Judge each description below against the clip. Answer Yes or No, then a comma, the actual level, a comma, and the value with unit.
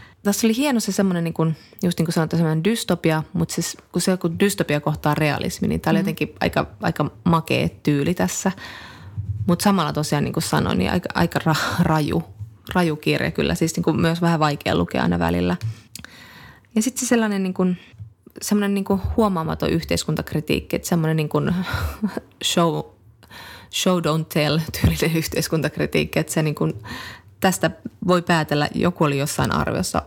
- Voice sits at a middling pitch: Yes, medium, 160 Hz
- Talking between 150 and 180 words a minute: Yes, fast, 155 wpm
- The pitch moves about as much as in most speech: No, wide, 7.6 semitones